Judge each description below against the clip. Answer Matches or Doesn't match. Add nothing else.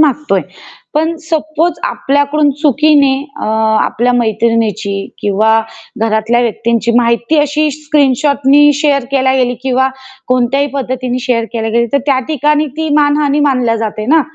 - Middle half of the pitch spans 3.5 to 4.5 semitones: Matches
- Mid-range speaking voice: Doesn't match